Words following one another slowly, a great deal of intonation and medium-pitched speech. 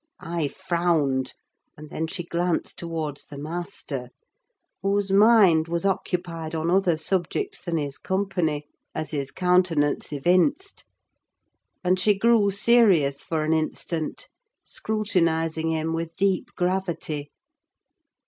No: slow, 115 wpm; average, 3.3 semitones; medium, 170 Hz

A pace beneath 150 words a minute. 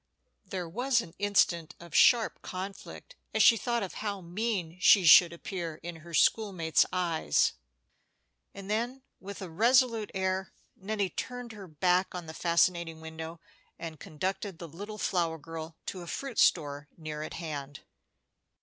No: average, 155 wpm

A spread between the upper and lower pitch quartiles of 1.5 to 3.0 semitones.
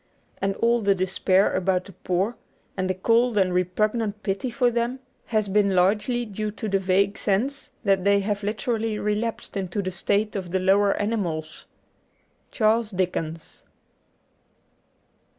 Yes: average, 2.7 semitones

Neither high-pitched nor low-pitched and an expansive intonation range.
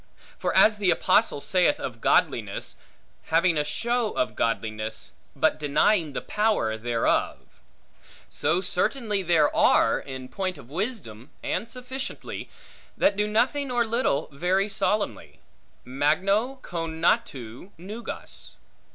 Yes: medium, 180 Hz; wide, 7.0 semitones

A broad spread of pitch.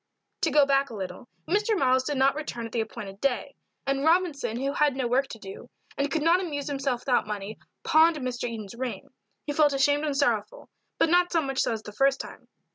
No: average, 3.9 semitones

